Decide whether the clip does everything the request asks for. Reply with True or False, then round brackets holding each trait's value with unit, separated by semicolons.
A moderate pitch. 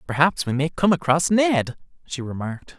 True (155 Hz)